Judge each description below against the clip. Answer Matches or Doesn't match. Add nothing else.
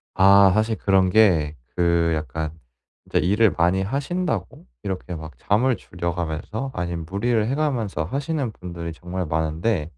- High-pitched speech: Doesn't match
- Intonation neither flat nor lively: Matches